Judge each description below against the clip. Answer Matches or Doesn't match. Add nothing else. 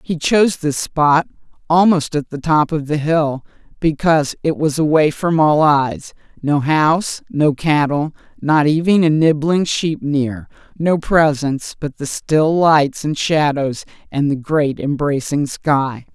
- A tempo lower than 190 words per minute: Matches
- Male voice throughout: Doesn't match